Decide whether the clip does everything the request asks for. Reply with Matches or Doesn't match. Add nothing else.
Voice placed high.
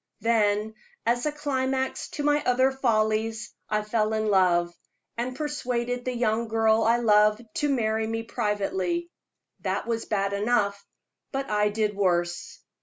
Matches